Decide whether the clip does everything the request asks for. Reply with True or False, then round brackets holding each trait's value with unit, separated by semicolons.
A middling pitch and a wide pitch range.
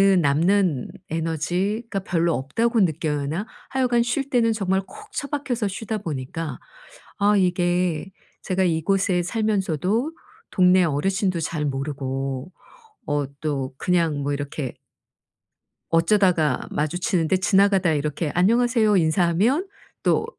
False (180 Hz; 5.0 semitones)